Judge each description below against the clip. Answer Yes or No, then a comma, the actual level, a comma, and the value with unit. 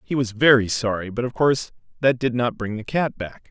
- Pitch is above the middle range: No, low, 120 Hz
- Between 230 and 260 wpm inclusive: Yes, fast, 240 wpm